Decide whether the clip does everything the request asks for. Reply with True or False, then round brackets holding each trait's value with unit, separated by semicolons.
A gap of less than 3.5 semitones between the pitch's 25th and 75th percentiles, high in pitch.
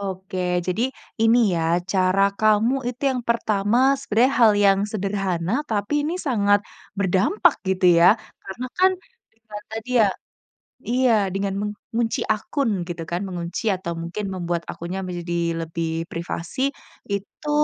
False (3.9 semitones; 200 Hz)